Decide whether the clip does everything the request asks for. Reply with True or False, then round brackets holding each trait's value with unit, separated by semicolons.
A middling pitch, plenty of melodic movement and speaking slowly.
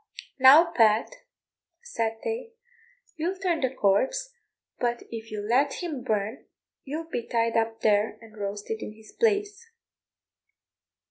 False (240 Hz; 7.6 semitones; 130 wpm)